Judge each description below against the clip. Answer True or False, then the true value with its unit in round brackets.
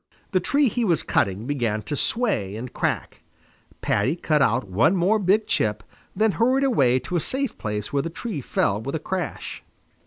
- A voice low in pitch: False (155 Hz)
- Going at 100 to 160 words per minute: False (185 wpm)